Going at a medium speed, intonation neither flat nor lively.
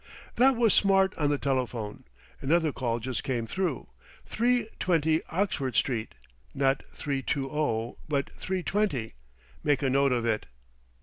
No: average, 145 wpm; wide, 6.3 semitones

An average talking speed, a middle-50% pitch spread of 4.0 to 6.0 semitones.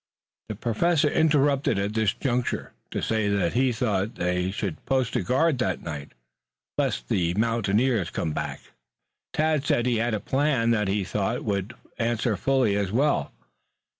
Yes: average, 160 wpm; average, 4.7 semitones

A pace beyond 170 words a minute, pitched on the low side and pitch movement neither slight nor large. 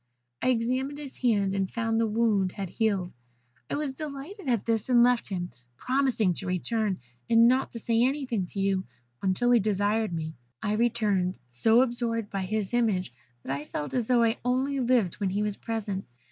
No: average, 190 wpm; high, 225 Hz; average, 3.9 semitones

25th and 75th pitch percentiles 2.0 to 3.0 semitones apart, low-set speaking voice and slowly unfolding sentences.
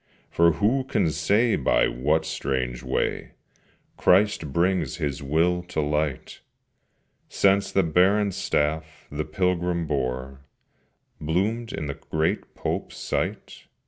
No: average, 4.0 semitones; very low, 80 Hz; slow, 115 wpm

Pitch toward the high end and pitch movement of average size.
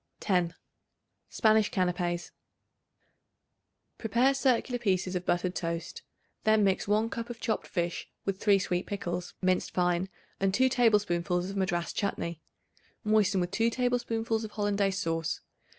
Yes: high, 195 Hz; average, 3.7 semitones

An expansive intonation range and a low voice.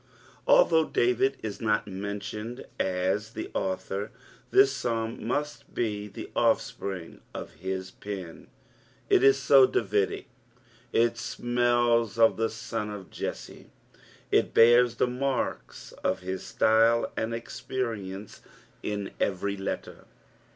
No: average, 3.3 semitones; low, 115 Hz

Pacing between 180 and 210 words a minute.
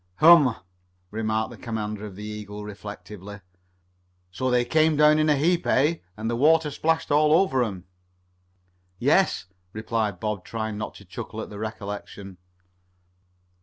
No: average, 145 wpm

